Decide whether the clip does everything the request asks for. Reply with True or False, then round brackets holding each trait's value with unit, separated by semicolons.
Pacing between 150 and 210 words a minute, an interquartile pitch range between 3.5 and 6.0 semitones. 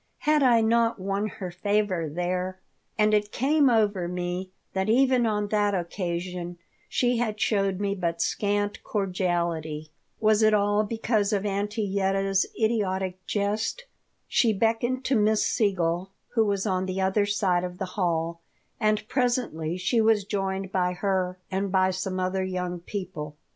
False (155 wpm; 2.8 semitones)